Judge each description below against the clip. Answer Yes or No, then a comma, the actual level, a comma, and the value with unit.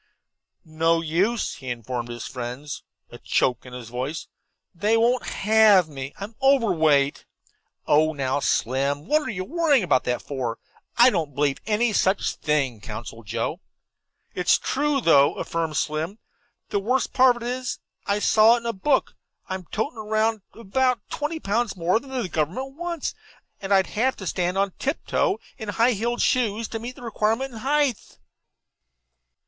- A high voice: Yes, high, 200 Hz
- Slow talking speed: No, average, 165 wpm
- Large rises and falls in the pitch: Yes, wide, 8.3 semitones